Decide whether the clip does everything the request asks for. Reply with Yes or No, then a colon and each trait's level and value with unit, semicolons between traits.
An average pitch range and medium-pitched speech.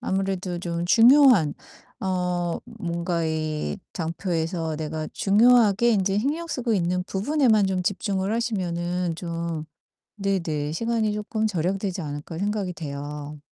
Yes: average, 3.9 semitones; medium, 180 Hz